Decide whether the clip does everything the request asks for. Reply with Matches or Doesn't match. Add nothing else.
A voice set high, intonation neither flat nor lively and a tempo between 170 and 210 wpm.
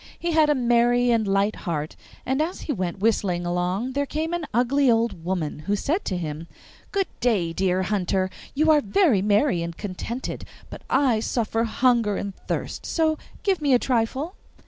Doesn't match